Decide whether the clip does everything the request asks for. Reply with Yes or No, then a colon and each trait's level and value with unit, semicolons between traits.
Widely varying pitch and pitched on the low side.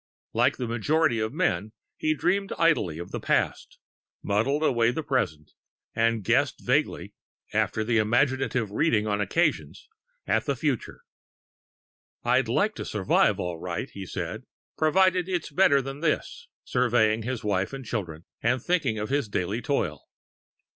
Yes: wide, 6.0 semitones; low, 120 Hz